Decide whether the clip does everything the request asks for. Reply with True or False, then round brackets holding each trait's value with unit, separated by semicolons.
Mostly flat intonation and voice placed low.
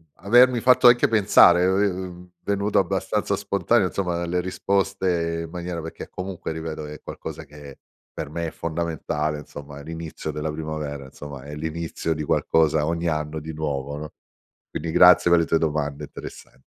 False (3.0 semitones; 80 Hz)